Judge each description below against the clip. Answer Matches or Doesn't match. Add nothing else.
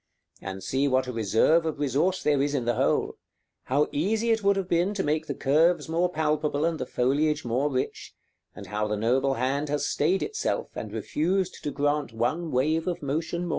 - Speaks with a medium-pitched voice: Matches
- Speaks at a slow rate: Doesn't match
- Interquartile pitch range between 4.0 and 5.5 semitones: Matches